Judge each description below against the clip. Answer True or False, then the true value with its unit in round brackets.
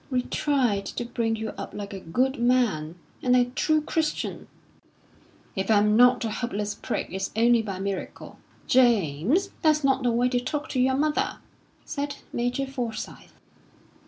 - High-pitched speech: True (245 Hz)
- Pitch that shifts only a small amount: False (4.1 semitones)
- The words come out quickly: False (160 wpm)